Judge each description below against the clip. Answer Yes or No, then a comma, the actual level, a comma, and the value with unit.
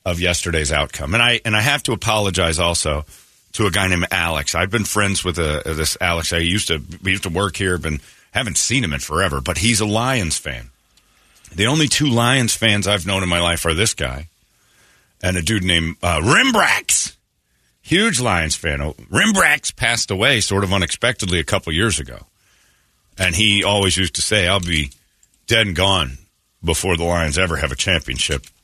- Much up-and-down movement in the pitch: No, average, 4.4 semitones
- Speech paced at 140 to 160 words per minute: No, average, 195 wpm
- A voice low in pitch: Yes, very low, 95 Hz